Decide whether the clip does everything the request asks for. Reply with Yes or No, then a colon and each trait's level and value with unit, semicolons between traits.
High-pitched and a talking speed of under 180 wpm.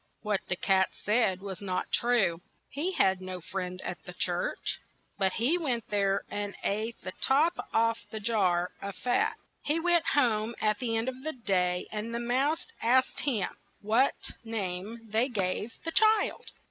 Yes: high, 225 Hz; average, 170 wpm